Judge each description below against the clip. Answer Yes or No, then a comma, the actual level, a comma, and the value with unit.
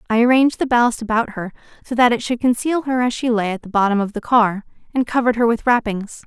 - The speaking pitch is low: No, high, 235 Hz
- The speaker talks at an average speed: No, fast, 250 wpm